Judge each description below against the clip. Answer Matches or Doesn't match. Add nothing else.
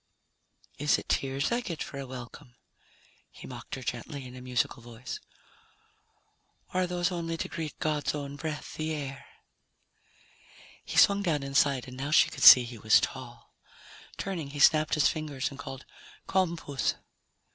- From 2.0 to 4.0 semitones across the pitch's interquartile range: Matches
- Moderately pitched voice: Matches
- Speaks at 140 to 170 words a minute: Matches